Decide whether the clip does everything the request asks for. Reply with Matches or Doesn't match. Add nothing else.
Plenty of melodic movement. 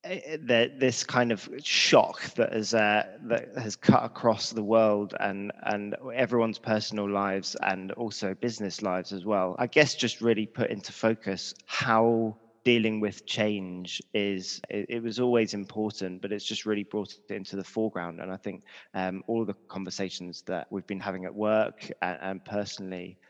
Doesn't match